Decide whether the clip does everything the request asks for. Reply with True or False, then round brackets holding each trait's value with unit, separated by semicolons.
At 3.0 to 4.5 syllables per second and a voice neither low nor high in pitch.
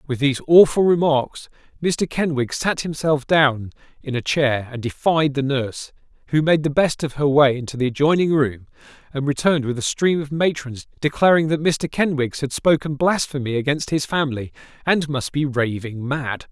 False (5.0 syllables/s; 145 Hz)